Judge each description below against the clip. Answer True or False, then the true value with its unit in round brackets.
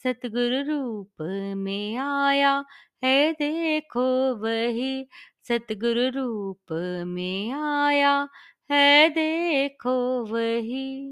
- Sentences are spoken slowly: True (75 wpm)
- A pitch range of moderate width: True (3.6 semitones)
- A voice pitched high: True (255 Hz)